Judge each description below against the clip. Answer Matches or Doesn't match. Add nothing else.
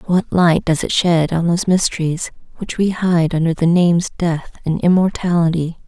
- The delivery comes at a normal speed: Matches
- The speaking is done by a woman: Matches